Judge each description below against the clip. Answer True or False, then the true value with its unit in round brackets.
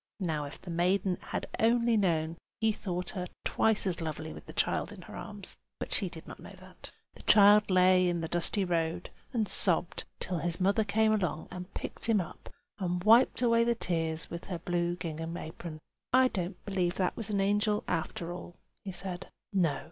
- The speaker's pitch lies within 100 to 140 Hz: False (180 Hz)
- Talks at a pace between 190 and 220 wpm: True (195 wpm)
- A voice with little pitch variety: False (3.3 semitones)